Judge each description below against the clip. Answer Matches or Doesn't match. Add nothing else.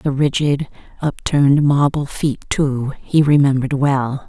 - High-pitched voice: Doesn't match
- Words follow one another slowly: Matches